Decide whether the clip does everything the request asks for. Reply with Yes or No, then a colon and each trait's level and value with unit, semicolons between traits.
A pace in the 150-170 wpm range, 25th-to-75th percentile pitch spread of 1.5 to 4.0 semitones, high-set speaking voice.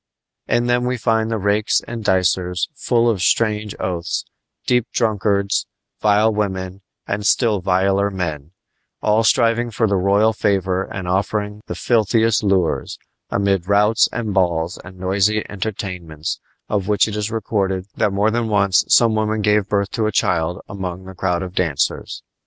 No: average, 160 wpm; average, 2.8 semitones; low, 100 Hz